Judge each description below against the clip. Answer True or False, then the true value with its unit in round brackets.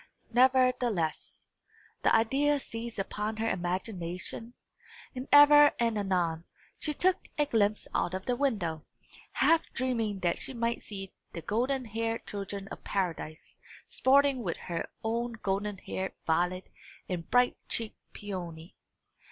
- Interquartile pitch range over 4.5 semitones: True (5.2 semitones)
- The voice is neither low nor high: False (220 Hz)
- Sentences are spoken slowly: True (130 wpm)